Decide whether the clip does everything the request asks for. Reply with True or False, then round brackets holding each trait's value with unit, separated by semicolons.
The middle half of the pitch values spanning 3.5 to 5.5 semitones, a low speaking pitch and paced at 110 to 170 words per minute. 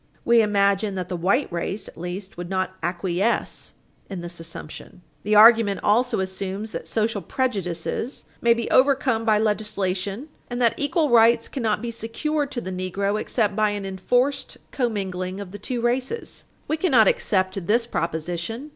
False (4.0 semitones; 210 Hz; 160 wpm)